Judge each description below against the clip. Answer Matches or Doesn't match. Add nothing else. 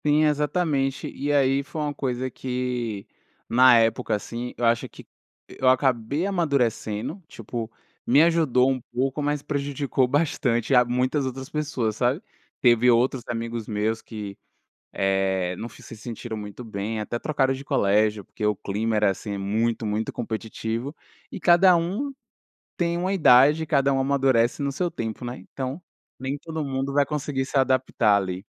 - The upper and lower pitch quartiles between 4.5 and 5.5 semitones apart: Doesn't match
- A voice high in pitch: Doesn't match